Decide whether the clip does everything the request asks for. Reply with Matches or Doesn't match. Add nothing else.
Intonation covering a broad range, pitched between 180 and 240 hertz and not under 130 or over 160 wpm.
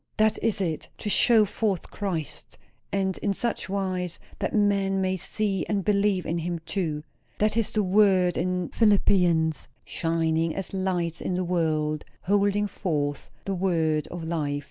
Doesn't match